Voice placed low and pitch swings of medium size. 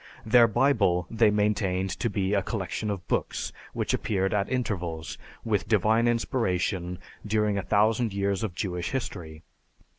Yes: low, 100 Hz; average, 3.2 semitones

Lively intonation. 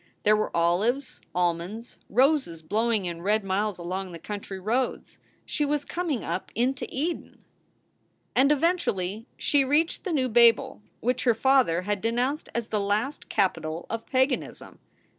Yes: wide, 5.8 semitones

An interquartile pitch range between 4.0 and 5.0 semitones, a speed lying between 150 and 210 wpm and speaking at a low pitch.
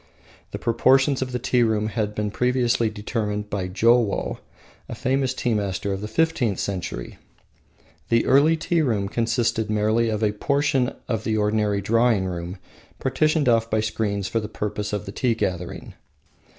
No: average, 3.0 semitones; average, 165 wpm; low, 110 Hz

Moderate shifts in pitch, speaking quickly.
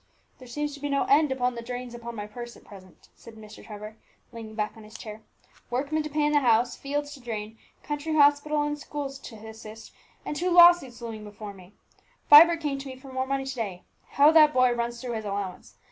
Yes: average, 4.8 semitones; fast, 225 wpm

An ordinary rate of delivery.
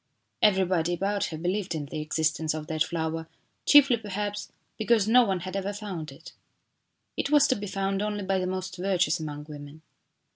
Yes: average, 180 wpm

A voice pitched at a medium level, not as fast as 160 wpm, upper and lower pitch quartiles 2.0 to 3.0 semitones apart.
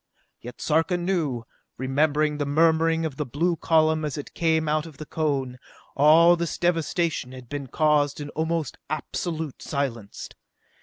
Yes: medium, 155 Hz; average, 150 wpm; narrow, 2.4 semitones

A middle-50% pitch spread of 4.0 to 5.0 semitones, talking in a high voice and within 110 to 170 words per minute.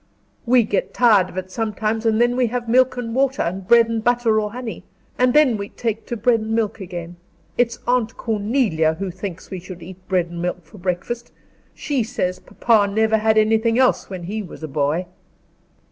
No: average, 4.3 semitones; high, 220 Hz; average, 200 wpm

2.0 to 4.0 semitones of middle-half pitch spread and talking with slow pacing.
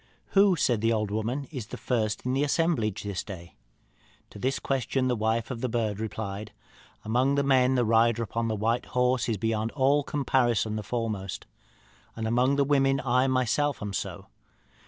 No: average, 3.4 semitones; average, 175 wpm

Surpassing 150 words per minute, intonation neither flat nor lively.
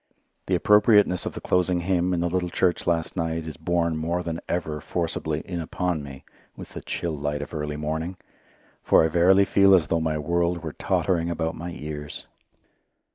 No: average, 185 wpm; narrow, 2.2 semitones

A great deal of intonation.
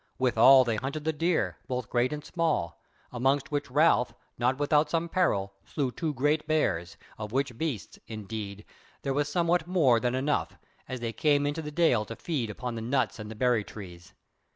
No: average, 4.8 semitones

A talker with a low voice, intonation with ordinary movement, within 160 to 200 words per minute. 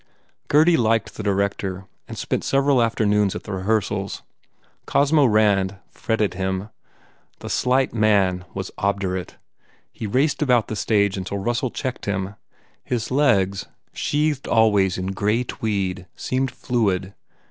No: low, 105 Hz; average, 4.1 semitones; slow, 135 wpm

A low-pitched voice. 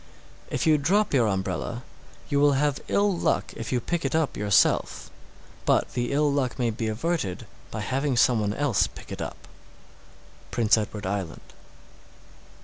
Yes: low, 125 Hz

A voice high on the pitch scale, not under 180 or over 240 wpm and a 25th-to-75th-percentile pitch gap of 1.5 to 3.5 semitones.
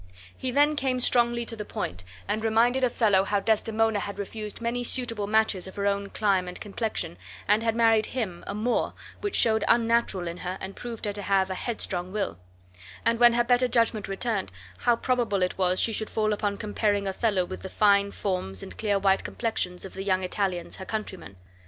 Yes: high, 210 Hz; average, 200 wpm; average, 3.2 semitones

